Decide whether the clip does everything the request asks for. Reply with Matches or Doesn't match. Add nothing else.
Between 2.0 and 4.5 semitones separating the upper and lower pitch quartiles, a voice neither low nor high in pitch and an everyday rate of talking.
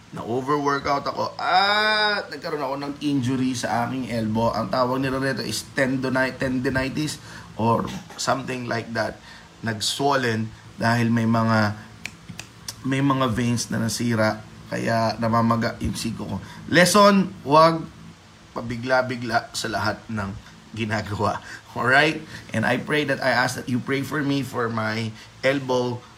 Doesn't match